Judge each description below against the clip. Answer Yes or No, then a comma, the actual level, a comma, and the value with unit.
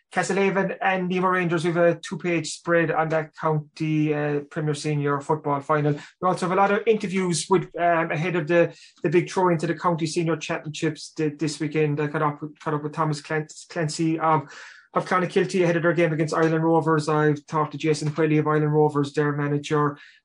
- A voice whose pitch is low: No, medium, 160 Hz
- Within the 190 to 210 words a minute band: Yes, average, 200 wpm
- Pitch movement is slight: Yes, narrow, 2.3 semitones